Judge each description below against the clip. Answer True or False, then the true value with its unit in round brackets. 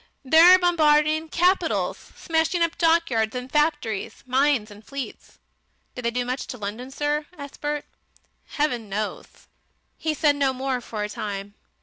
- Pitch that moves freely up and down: False (5.0 semitones)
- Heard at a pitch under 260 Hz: False (280 Hz)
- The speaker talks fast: False (145 wpm)